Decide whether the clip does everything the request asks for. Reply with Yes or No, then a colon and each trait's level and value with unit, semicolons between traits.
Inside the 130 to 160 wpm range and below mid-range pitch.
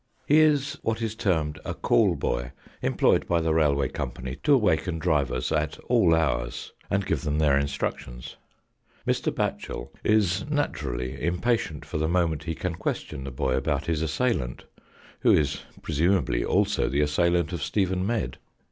Yes: average, 155 wpm; very low, 80 Hz